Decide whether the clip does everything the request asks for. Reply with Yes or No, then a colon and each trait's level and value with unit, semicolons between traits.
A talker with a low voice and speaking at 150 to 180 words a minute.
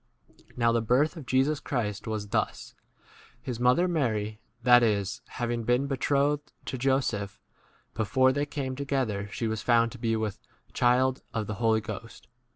Yes: low, 120 Hz; average, 170 wpm